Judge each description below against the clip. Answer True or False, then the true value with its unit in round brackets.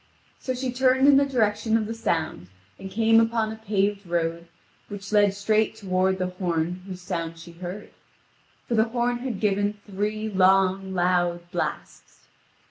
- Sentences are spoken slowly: False (160 wpm)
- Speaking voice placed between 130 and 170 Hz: False (200 Hz)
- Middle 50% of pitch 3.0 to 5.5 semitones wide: True (3.4 semitones)